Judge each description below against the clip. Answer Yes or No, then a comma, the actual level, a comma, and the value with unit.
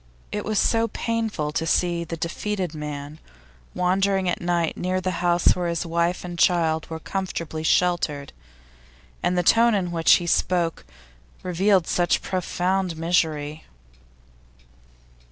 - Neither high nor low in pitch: Yes, medium, 175 Hz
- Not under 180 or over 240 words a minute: No, slow, 135 wpm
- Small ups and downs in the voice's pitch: Yes, narrow, 2.2 semitones